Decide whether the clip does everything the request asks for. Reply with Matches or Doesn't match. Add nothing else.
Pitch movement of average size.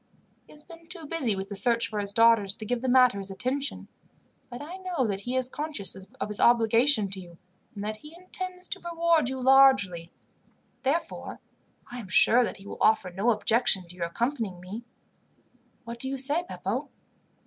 Doesn't match